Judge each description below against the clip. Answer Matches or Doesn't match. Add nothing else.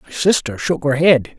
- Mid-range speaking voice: Matches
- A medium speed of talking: Doesn't match